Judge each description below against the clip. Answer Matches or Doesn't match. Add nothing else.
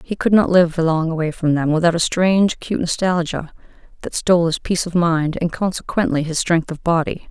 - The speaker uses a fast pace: Matches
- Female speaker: Matches